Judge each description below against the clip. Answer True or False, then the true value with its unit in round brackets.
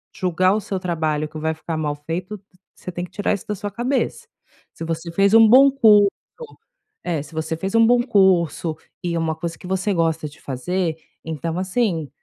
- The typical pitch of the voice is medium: True (180 Hz)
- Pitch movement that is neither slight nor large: True (4.2 semitones)